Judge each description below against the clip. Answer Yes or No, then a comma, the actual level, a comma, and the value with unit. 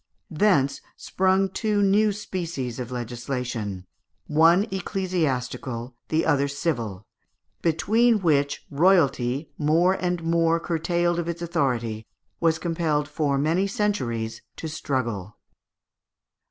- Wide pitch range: Yes, wide, 5.8 semitones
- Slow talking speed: Yes, slow, 105 wpm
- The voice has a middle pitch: Yes, medium, 160 Hz